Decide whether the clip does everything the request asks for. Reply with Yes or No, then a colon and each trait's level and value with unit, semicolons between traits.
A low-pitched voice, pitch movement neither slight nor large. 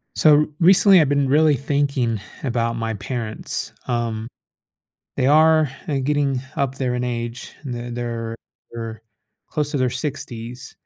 Yes: low, 125 Hz; average, 3.6 semitones